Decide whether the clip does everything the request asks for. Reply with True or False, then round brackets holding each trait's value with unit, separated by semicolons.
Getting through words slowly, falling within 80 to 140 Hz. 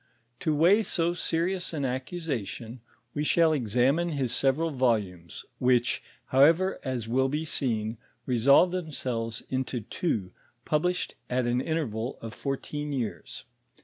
True (125 wpm; 135 Hz)